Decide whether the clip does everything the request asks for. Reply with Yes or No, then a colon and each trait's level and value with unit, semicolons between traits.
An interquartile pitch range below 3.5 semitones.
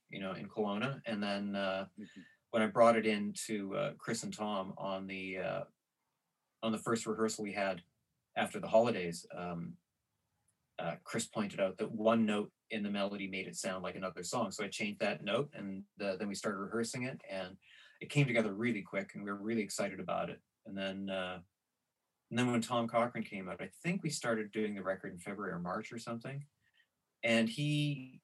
Yes: average, 3.1 semitones